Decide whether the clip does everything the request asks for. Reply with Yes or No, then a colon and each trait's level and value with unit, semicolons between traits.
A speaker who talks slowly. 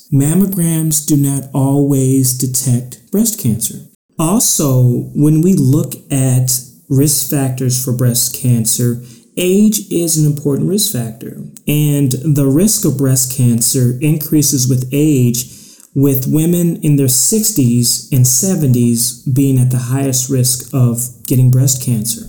Yes: slow, 130 wpm